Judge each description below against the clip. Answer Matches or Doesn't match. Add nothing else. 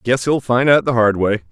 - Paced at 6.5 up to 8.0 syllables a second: Doesn't match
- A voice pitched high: Doesn't match